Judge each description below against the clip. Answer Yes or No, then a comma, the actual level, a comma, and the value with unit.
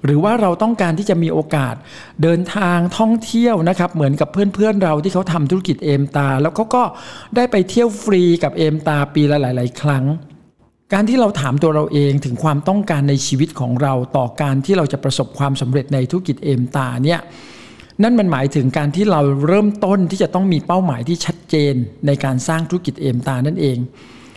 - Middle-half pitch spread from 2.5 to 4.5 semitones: No, average, 4.9 semitones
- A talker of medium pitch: Yes, medium, 155 Hz